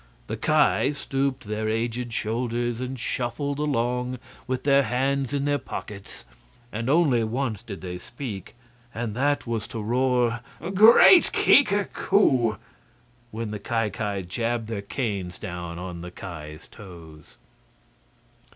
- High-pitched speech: No, low, 115 Hz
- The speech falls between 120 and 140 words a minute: Yes, slow, 135 wpm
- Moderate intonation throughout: Yes, average, 4.2 semitones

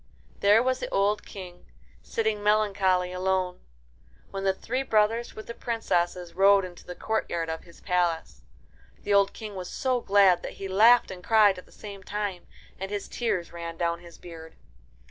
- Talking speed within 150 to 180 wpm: Yes, average, 175 wpm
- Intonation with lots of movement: No, average, 3.0 semitones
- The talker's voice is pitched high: Yes, high, 195 Hz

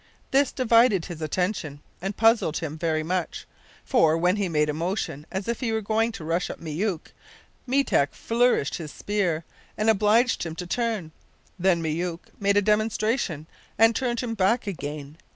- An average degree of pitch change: No, wide, 5.7 semitones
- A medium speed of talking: Yes, average, 170 wpm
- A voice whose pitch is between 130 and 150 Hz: No, high, 190 Hz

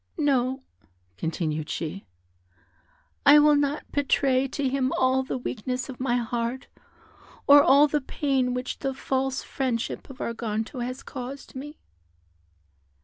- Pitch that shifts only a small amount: Yes, narrow, 2.1 semitones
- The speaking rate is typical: No, slow, 130 wpm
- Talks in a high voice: Yes, very high, 260 Hz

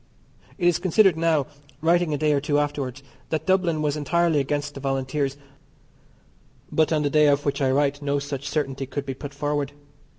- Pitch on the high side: No, medium, 145 Hz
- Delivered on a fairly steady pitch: Yes, narrow, 1.9 semitones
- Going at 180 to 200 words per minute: Yes, average, 190 wpm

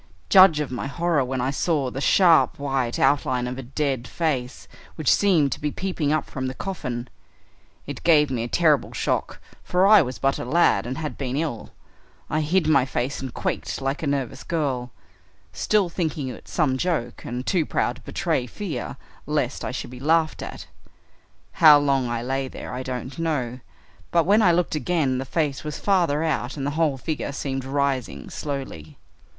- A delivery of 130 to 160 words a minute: No, average, 190 wpm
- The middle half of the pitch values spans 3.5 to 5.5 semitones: Yes, average, 3.9 semitones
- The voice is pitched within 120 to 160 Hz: Yes, medium, 140 Hz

